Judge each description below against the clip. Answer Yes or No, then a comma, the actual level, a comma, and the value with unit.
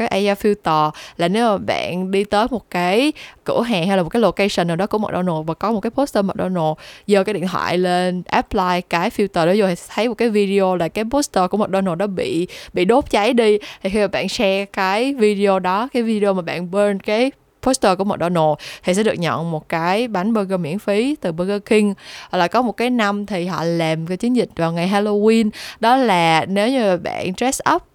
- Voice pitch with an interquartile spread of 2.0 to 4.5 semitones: Yes, average, 3.5 semitones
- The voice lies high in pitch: Yes, high, 200 Hz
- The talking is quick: No, average, 230 wpm